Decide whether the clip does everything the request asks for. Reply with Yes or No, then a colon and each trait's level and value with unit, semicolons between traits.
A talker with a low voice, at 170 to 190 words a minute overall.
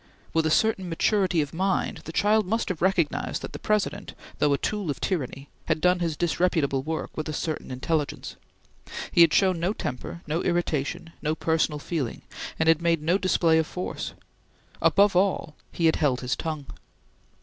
No: medium, 165 Hz; average, 180 wpm